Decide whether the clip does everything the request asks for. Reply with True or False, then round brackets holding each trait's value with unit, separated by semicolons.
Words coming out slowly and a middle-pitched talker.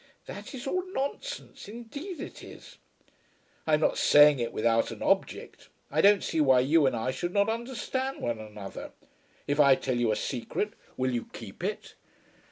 False (175 wpm; 150 Hz)